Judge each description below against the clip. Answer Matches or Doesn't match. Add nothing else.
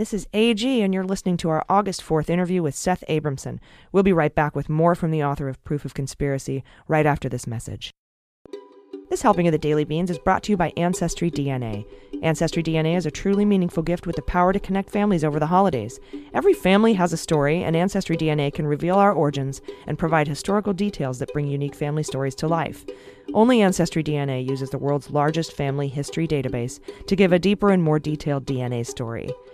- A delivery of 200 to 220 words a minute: Matches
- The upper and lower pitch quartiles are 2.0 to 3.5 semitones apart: Doesn't match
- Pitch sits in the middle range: Matches